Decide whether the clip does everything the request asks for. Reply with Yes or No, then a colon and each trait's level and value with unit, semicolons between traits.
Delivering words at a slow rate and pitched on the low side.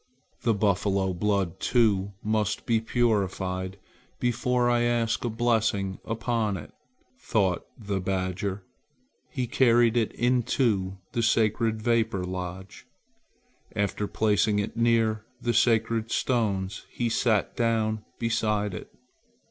Yes: slow, 115 wpm; low, 110 Hz